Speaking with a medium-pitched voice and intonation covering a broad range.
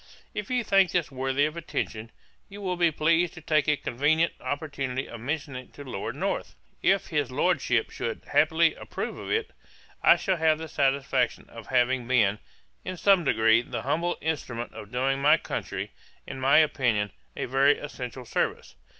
No: medium, 145 Hz; average, 4.3 semitones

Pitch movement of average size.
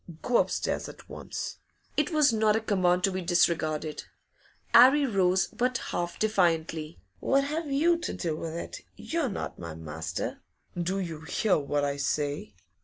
No: wide, 8.0 semitones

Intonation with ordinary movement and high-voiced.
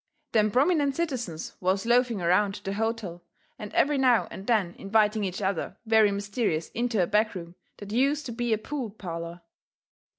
Yes: average, 3.9 semitones; high, 215 Hz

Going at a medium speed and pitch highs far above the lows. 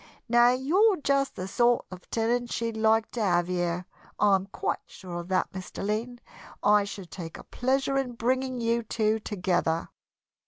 No: average, 165 wpm; average, 4.6 semitones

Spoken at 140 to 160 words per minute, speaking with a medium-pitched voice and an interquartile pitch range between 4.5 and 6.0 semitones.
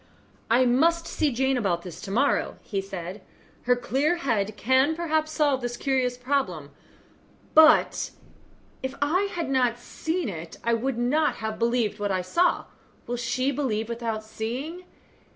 No: average, 150 wpm; high, 245 Hz; average, 4.8 semitones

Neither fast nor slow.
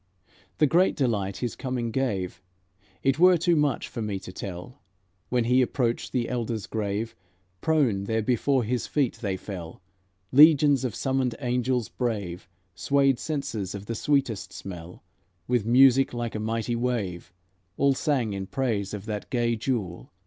Yes: average, 155 wpm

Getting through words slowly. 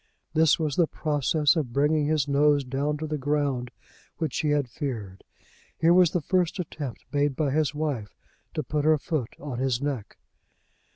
No: average, 175 wpm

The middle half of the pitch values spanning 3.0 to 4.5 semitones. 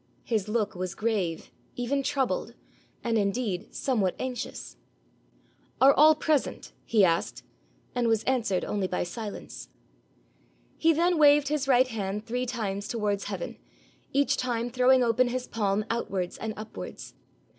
Yes: average, 4.1 semitones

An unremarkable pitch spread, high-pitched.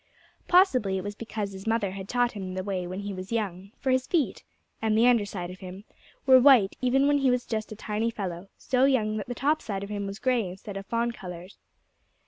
Yes: average, 4.2 semitones; high, 210 Hz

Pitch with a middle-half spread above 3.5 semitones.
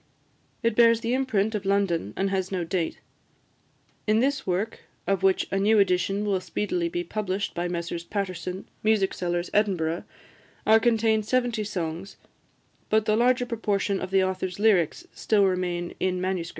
No: average, 3.1 semitones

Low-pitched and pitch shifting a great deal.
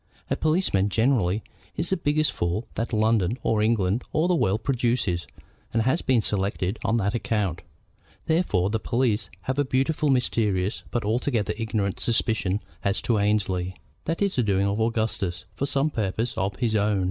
No: low, 110 Hz; average, 4.3 semitones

